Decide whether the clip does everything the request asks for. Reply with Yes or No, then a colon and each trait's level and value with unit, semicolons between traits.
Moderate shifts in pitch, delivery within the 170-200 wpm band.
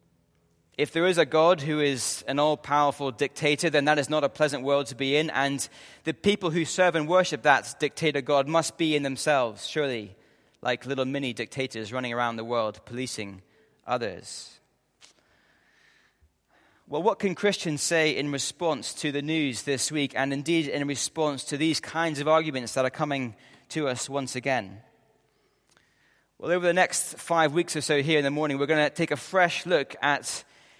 Yes: average, 3.4 semitones; average, 185 wpm